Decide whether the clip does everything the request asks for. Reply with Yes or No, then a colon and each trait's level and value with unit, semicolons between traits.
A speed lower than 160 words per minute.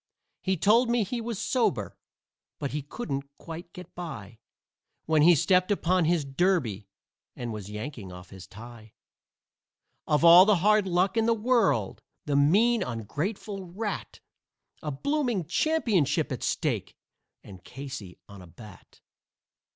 Yes: average, 140 wpm